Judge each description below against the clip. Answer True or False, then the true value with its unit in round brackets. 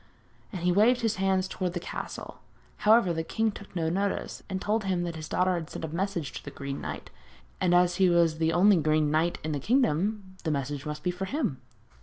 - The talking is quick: True (225 wpm)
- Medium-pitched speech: True (180 Hz)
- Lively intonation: False (3.5 semitones)